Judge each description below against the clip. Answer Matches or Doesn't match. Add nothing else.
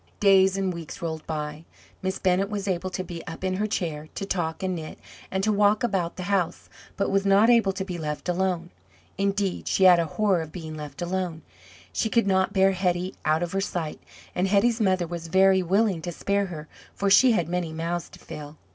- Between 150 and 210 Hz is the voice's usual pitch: Matches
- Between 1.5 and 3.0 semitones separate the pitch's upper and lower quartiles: Matches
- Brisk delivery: Matches